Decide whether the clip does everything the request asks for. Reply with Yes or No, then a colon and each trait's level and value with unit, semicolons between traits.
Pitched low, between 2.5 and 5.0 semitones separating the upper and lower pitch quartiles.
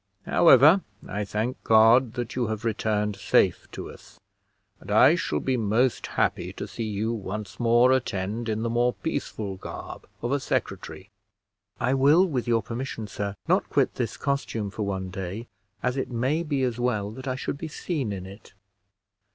Yes: low, 115 Hz; average, 3.8 semitones